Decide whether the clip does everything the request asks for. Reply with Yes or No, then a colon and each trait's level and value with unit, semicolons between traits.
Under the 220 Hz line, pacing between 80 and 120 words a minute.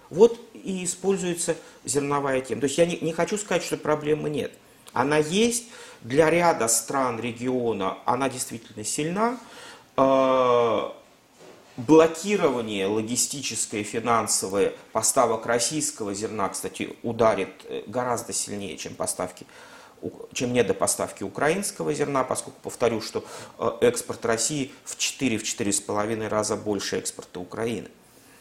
Yes: medium, 140 Hz; slow, 110 wpm